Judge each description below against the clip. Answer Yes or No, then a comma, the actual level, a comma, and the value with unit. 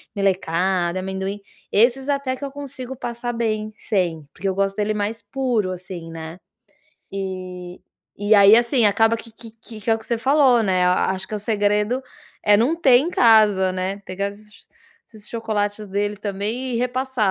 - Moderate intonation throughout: Yes, average, 3.7 semitones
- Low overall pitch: No, high, 210 Hz